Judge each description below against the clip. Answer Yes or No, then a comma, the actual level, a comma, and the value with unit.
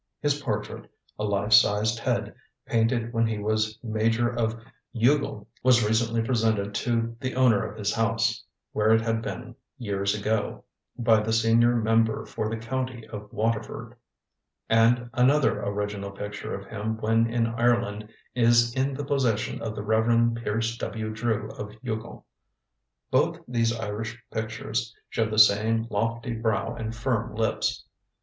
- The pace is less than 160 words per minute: Yes, average, 150 wpm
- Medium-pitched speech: No, low, 115 Hz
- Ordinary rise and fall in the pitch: No, narrow, 1.5 semitones